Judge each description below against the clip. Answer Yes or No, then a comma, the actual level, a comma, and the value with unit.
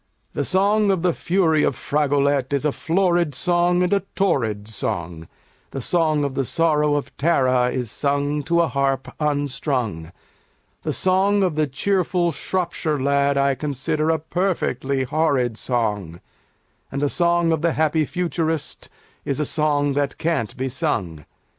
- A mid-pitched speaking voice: Yes, medium, 150 Hz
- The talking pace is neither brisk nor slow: Yes, average, 155 wpm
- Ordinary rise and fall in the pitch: Yes, average, 4.1 semitones